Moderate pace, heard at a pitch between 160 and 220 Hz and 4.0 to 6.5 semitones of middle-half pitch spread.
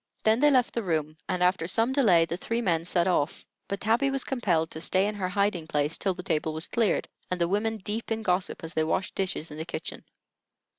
No: fast, 235 wpm; medium, 185 Hz; average, 5.1 semitones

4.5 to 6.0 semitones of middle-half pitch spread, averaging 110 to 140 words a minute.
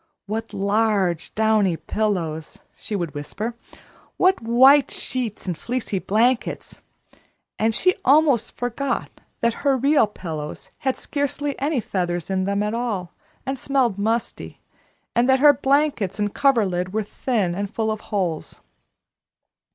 Yes: average, 5.1 semitones; slow, 135 wpm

